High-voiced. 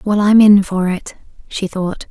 Yes: high, 195 Hz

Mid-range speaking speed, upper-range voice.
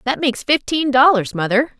Yes: average, 165 wpm; very high, 260 Hz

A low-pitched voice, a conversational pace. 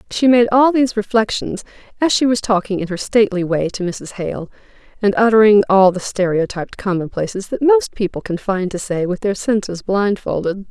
No: high, 205 Hz; average, 185 wpm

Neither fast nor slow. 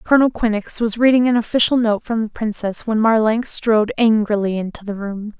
Yes: average, 190 wpm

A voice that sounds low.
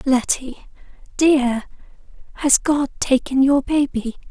No: very high, 270 Hz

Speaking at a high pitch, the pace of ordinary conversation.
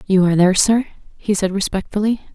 Yes: high, 200 Hz; average, 180 wpm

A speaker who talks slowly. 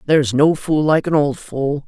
No: fast, 225 wpm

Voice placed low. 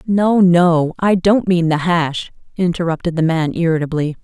No: medium, 170 Hz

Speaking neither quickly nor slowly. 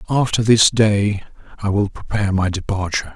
Yes: average, 150 wpm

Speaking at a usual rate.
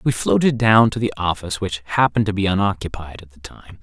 No: fast, 220 wpm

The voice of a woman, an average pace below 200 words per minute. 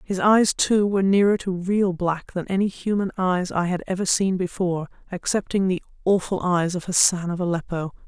Yes: female; average, 180 wpm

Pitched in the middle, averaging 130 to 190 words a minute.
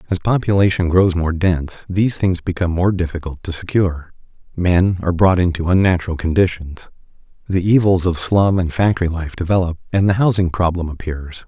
No: very low, 90 Hz; average, 160 wpm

